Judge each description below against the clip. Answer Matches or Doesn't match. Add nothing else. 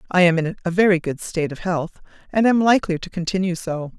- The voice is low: Doesn't match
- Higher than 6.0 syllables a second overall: Matches